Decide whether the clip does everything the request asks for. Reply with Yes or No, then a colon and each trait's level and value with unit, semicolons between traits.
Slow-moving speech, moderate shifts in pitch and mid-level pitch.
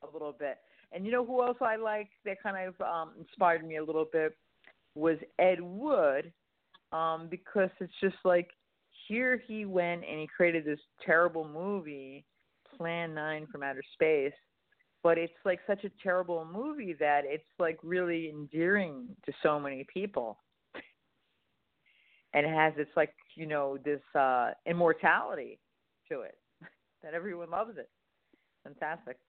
No: average, 150 wpm; average, 4.1 semitones; medium, 170 Hz